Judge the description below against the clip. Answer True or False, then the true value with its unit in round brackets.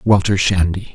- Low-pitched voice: True (95 Hz)